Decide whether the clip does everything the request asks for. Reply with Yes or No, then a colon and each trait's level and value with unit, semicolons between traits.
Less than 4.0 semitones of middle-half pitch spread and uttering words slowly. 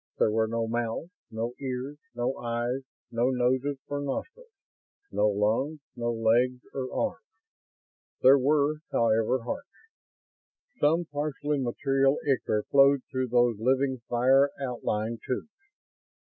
Yes: average, 3.1 semitones; slow, 120 wpm